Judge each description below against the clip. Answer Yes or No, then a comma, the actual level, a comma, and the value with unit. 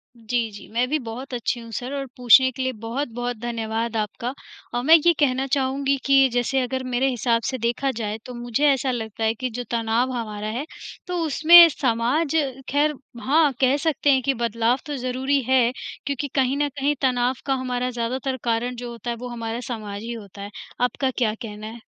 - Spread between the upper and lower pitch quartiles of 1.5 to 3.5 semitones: Yes, average, 2.7 semitones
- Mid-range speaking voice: No, high, 245 Hz